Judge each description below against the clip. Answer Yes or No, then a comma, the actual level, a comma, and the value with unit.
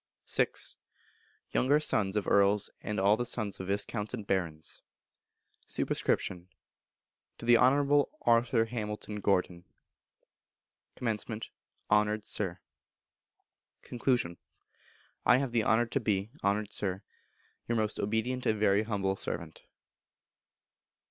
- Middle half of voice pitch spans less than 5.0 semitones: Yes, average, 3.0 semitones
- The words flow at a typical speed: No, slow, 110 wpm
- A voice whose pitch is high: No, low, 105 Hz